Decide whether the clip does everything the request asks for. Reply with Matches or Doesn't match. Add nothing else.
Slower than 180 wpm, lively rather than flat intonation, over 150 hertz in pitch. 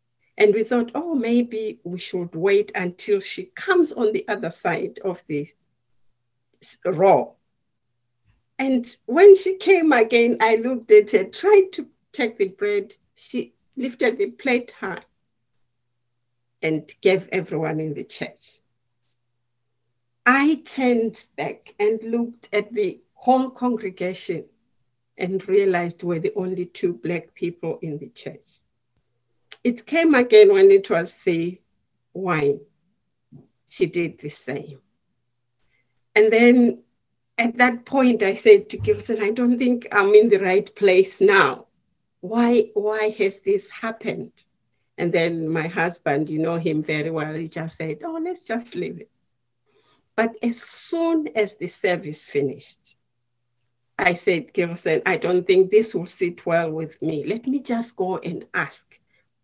Matches